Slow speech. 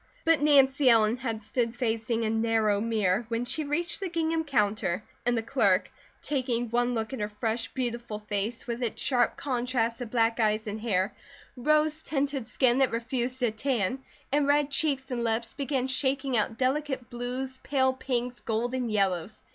No: average, 170 wpm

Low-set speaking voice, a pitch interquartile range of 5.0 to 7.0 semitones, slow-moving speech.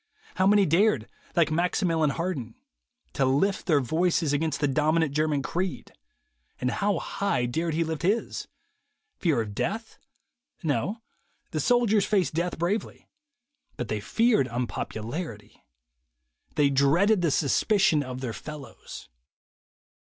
No: medium, 160 Hz; wide, 5.5 semitones; slow, 130 wpm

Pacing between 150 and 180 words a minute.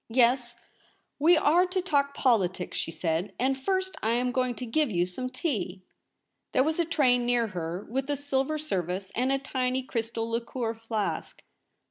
Yes: average, 175 wpm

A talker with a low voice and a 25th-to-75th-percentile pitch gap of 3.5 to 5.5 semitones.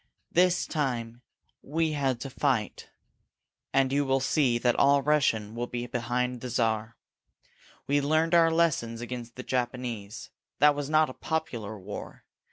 Yes: low, 130 Hz; average, 3.8 semitones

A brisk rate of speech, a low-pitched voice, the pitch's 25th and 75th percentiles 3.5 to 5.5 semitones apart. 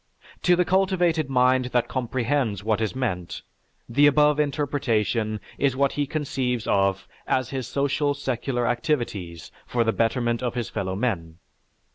No: average, 140 wpm; low, 125 Hz; average, 4.1 semitones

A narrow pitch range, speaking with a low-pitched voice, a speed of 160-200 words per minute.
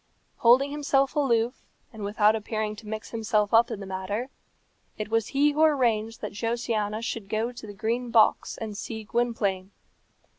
No: narrow, 2.2 semitones; high, 225 Hz; average, 170 wpm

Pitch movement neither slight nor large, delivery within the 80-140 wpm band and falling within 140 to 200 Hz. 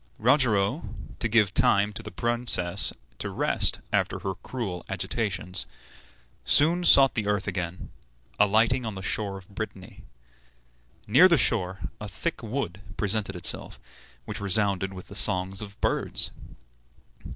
No: average, 3.3 semitones; slow, 135 wpm; low, 105 Hz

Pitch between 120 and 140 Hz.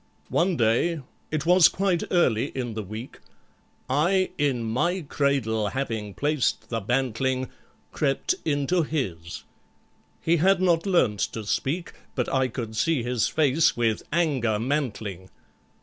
Yes: low, 135 Hz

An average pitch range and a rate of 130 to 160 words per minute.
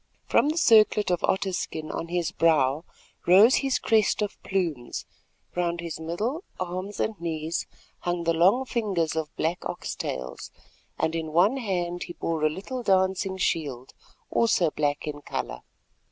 Yes: average, 3.8 semitones; average, 155 wpm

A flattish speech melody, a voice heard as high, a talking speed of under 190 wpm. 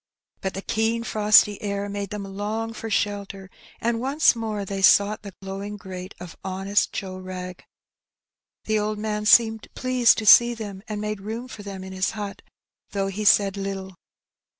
Yes: narrow, 2.0 semitones; high, 205 Hz; average, 175 wpm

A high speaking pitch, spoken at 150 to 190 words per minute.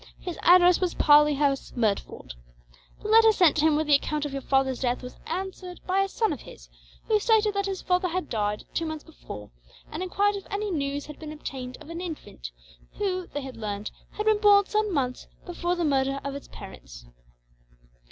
No: very high, 315 Hz; average, 200 wpm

